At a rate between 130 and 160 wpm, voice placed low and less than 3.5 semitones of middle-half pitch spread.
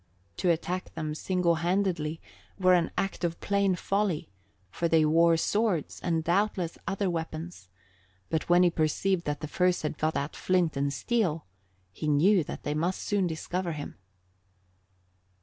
No: average, 155 wpm; medium, 170 Hz; average, 2.8 semitones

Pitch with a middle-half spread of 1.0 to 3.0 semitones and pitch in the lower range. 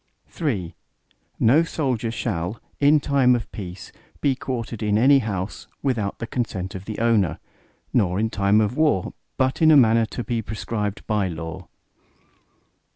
No: average, 4.5 semitones; low, 110 Hz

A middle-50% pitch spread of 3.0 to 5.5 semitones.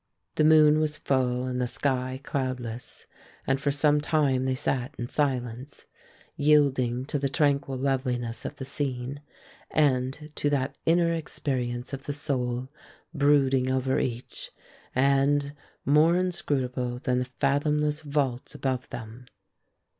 No: narrow, 2.4 semitones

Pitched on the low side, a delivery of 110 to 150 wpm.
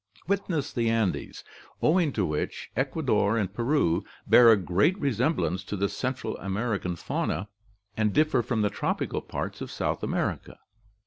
Yes: low, 115 Hz; average, 145 wpm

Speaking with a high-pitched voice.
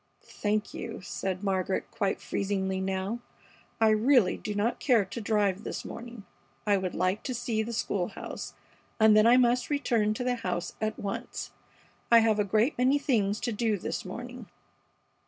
Yes: high, 215 Hz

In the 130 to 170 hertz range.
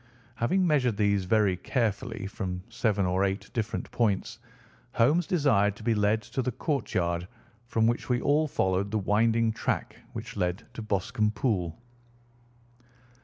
No: low, 110 Hz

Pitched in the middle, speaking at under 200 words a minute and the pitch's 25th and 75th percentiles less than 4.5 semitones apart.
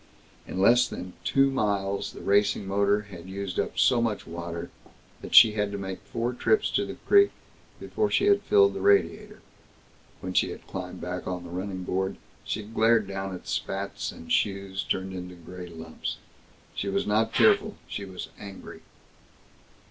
No: low, 100 Hz; average, 170 wpm; average, 3.6 semitones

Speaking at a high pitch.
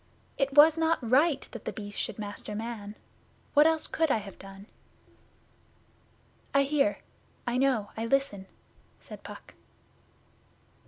Yes: very high, 255 Hz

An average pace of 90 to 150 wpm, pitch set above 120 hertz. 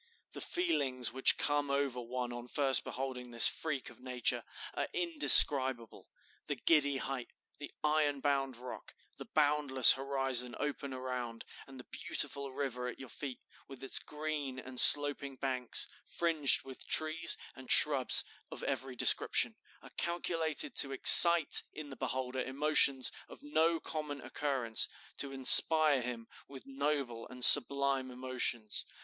Yes: average, 140 wpm; low, 135 Hz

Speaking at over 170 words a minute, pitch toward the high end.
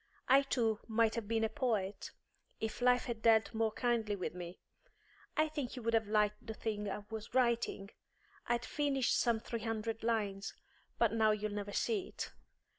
Yes: average, 180 wpm; high, 225 Hz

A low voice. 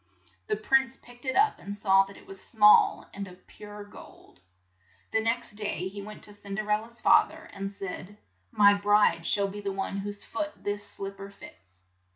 No: high, 205 Hz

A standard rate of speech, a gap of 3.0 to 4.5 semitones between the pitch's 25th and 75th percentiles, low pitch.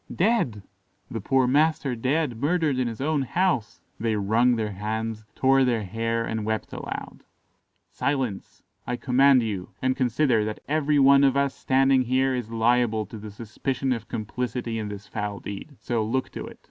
Yes: average, 170 wpm; average, 3.5 semitones; low, 120 Hz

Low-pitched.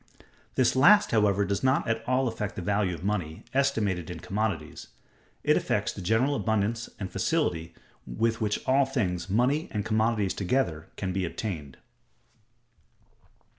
Yes: low, 105 Hz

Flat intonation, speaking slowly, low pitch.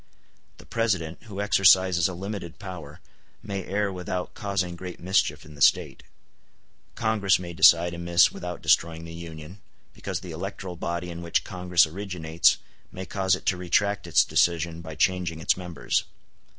No: narrow, 2.3 semitones; average, 155 wpm; very low, 90 Hz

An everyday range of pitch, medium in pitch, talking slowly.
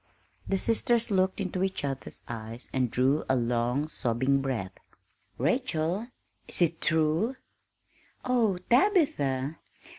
No: wide, 7.1 semitones; medium, 155 Hz; slow, 115 wpm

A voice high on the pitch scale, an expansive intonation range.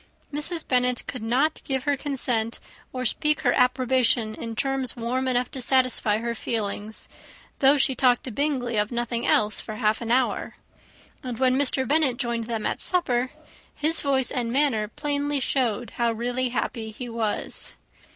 No: very high, 250 Hz; average, 2.7 semitones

